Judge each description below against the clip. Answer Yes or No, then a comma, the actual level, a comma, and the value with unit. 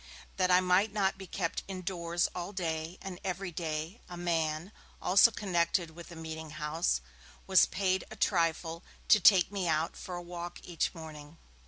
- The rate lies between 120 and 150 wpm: No, average, 165 wpm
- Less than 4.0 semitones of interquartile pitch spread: Yes, narrow, 2.6 semitones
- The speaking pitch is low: No, medium, 175 Hz